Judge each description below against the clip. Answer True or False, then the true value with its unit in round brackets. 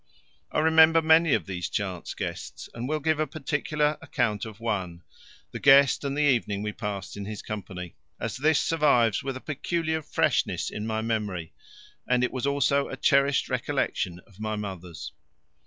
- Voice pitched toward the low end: True (120 Hz)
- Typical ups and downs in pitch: False (6.3 semitones)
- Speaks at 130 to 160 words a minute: False (170 wpm)